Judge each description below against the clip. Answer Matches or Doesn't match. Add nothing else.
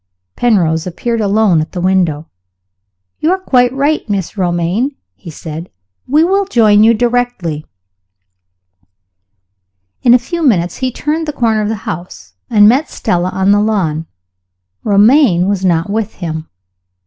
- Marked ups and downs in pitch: Matches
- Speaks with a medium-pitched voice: Doesn't match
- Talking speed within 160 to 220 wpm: Doesn't match